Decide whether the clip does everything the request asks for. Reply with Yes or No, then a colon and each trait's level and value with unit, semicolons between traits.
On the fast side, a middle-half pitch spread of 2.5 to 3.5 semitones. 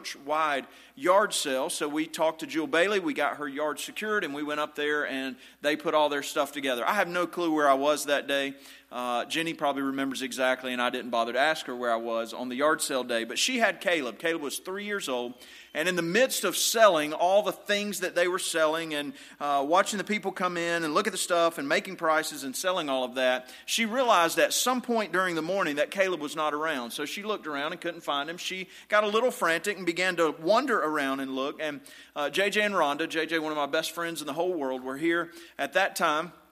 No: fast, 245 wpm; average, 4.9 semitones